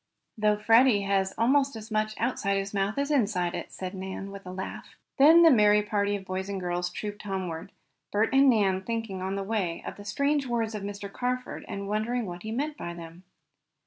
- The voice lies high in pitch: Yes, high, 205 Hz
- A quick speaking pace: Yes, fast, 210 wpm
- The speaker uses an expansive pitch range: No, average, 3.1 semitones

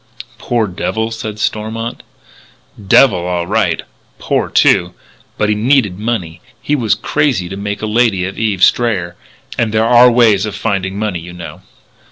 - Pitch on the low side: Yes, low, 105 Hz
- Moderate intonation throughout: Yes, average, 3.5 semitones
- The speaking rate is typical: Yes, average, 160 wpm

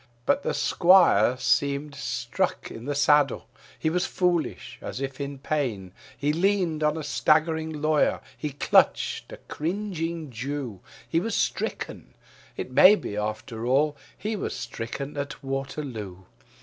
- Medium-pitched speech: Yes, medium, 145 Hz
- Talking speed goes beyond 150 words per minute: No, average, 140 wpm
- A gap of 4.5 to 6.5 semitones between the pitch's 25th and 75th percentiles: No, average, 3.5 semitones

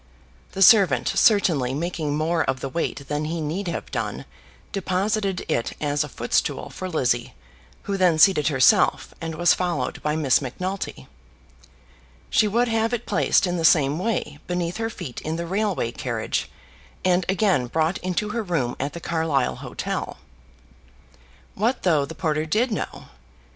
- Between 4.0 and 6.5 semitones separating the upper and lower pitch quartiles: Yes, average, 4.7 semitones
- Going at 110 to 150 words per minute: No, average, 160 wpm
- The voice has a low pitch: No, medium, 170 Hz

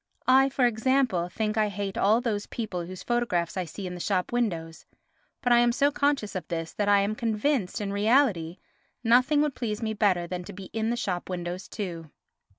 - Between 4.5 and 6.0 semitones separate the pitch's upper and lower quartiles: Yes, average, 4.8 semitones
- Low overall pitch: No, high, 210 Hz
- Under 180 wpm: No, fast, 205 wpm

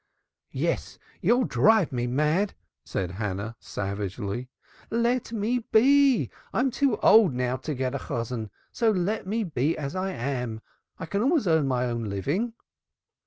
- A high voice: No, medium, 150 Hz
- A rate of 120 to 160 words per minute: Yes, average, 150 wpm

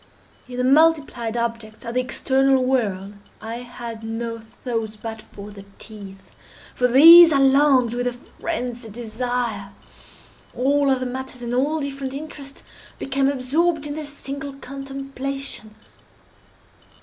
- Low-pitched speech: No, very high, 255 Hz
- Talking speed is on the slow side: Yes, slow, 130 wpm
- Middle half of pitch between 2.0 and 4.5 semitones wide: Yes, average, 3.1 semitones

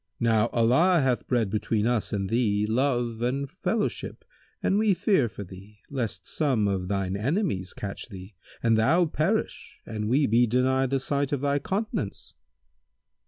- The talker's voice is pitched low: Yes, low, 120 Hz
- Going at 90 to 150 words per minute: No, average, 160 wpm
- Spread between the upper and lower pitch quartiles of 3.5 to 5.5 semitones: Yes, average, 5.1 semitones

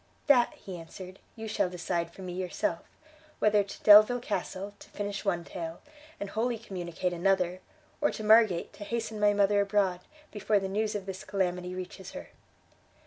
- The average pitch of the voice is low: No, high, 195 Hz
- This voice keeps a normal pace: Yes, average, 170 wpm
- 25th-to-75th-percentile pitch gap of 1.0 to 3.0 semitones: Yes, narrow, 2.6 semitones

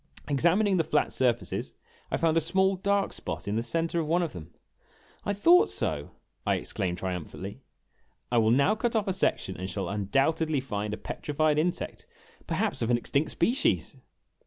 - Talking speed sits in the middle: Yes, average, 175 wpm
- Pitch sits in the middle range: Yes, medium, 155 Hz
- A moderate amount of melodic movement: No, wide, 8.6 semitones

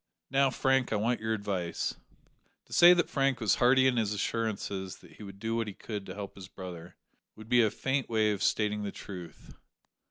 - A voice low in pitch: Yes, low, 110 Hz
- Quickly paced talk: Yes, fast, 210 wpm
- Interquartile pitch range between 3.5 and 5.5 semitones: Yes, average, 3.8 semitones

